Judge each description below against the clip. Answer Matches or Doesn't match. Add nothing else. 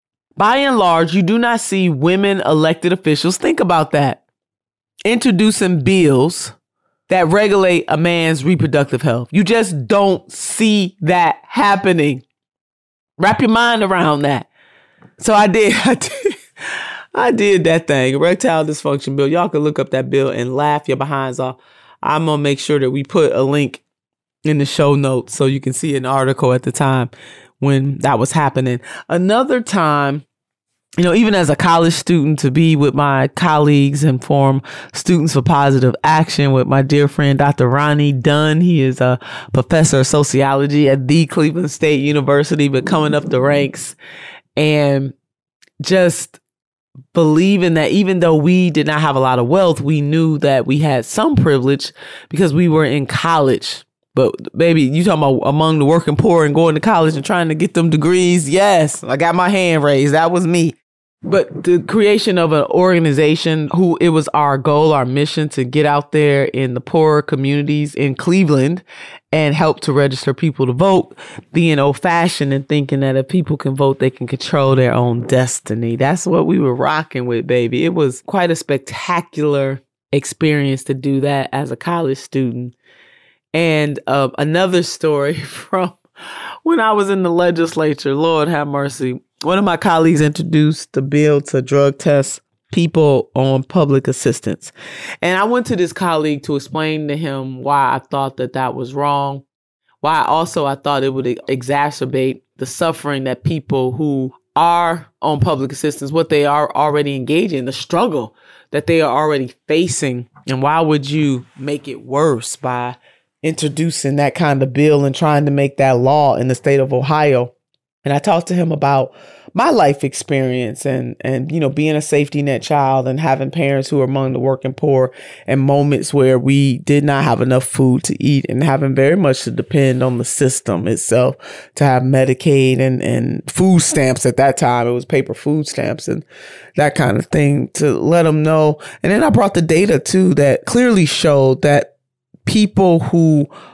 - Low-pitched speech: Doesn't match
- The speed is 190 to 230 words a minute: Doesn't match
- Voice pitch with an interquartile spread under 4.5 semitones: Matches